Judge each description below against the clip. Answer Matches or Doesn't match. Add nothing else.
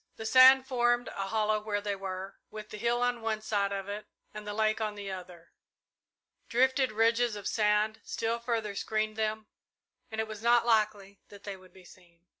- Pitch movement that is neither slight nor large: Doesn't match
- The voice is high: Matches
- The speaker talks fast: Doesn't match